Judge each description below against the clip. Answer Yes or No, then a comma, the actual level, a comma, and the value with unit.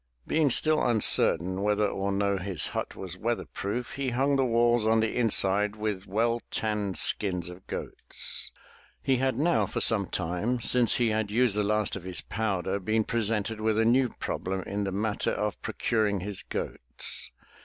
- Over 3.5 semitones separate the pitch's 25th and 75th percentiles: No, average, 3.1 semitones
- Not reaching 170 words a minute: No, average, 180 wpm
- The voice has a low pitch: Yes, low, 105 Hz